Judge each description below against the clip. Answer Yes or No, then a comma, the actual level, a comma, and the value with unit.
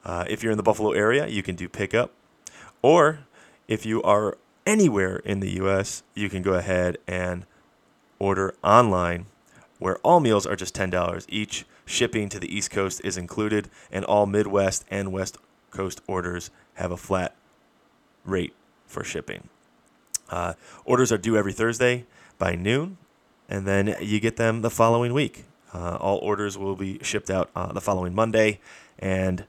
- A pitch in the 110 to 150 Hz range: No, low, 100 Hz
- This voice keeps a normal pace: Yes, average, 165 wpm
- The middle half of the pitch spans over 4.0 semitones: No, average, 2.9 semitones